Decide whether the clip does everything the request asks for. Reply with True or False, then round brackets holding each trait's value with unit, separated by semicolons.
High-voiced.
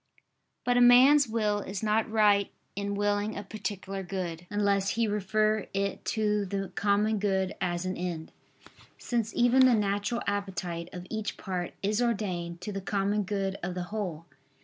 True (200 Hz)